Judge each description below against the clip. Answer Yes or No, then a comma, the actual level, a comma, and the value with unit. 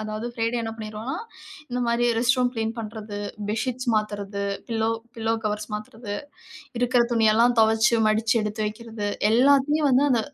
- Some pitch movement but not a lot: No, narrow, 2.2 semitones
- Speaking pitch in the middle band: No, high, 225 Hz